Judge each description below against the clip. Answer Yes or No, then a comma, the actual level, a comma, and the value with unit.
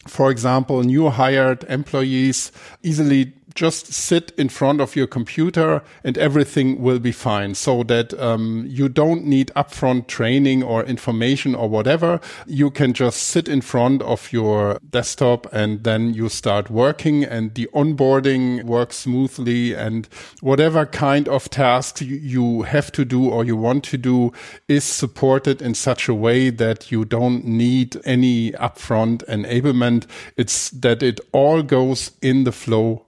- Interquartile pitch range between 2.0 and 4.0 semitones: Yes, average, 2.9 semitones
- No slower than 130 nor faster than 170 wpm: Yes, average, 155 wpm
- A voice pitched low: Yes, low, 130 Hz